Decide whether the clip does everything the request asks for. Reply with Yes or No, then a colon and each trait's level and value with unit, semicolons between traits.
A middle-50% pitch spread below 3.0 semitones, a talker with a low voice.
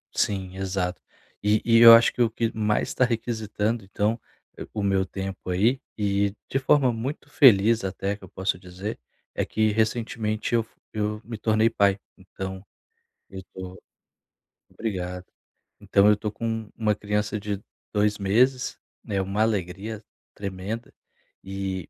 Yes: narrow, 2.6 semitones; low, 105 Hz